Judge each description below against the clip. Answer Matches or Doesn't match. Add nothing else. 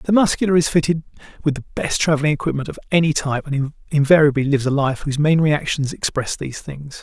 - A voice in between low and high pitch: Matches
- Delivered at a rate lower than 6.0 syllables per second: Doesn't match